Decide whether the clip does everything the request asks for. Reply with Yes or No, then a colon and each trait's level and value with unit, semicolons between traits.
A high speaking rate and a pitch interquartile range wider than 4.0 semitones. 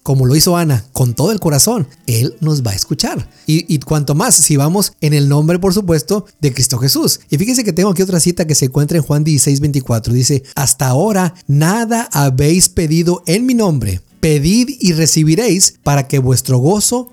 Yes: fast, 195 wpm; average, 4.6 semitones